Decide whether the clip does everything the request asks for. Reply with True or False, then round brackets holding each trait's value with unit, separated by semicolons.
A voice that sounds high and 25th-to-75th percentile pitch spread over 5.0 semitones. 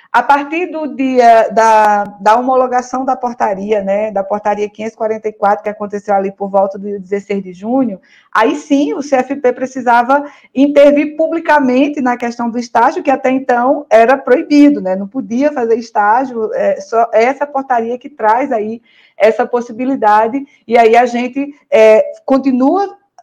False (245 Hz; 4.3 semitones)